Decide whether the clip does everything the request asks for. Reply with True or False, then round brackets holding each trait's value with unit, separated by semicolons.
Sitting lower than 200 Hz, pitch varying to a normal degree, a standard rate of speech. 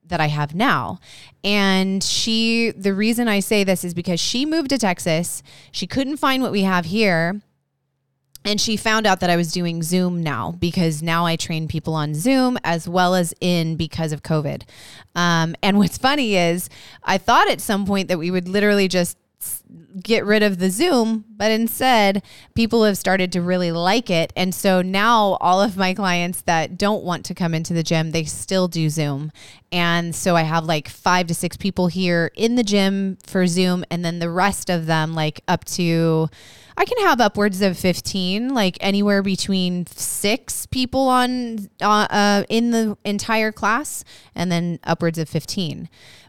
True (185 Hz; 3.7 semitones; 185 wpm)